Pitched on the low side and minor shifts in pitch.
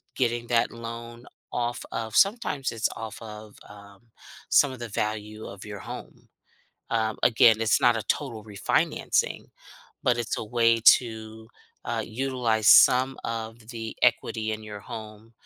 Yes: low, 115 Hz; narrow, 1.6 semitones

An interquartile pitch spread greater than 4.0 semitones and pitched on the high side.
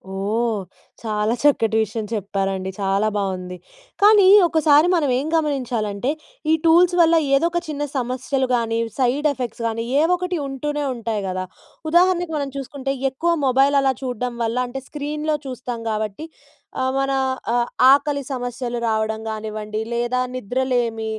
Yes: average, 4.9 semitones; very high, 250 Hz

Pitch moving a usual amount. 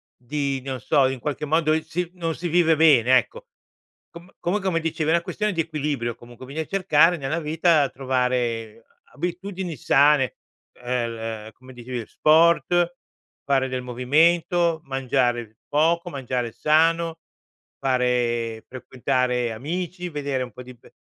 Yes: average, 4.9 semitones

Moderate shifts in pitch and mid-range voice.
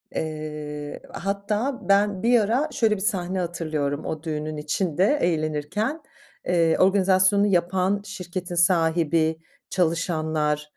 Yes: average, 4.1 semitones; medium, 175 Hz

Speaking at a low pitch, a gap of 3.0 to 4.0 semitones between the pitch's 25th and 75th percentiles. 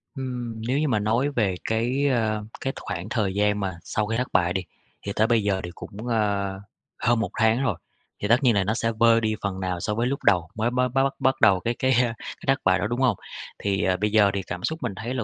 Yes: low, 110 Hz; average, 3.6 semitones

